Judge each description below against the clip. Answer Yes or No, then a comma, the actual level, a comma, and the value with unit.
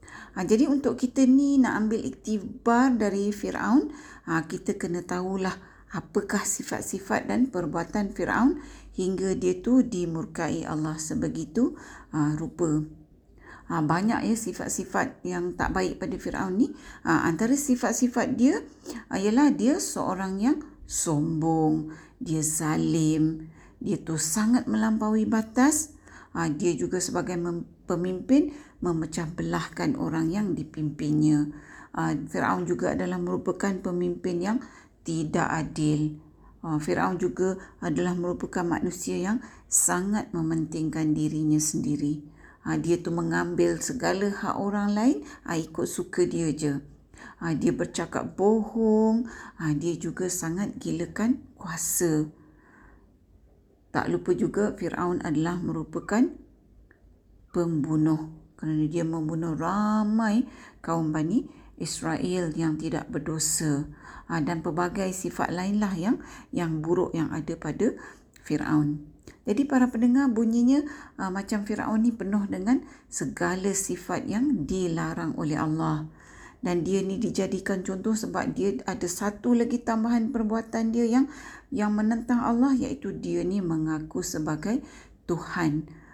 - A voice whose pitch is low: No, medium, 185 Hz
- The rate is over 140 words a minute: No, average, 120 wpm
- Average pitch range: No, wide, 6.2 semitones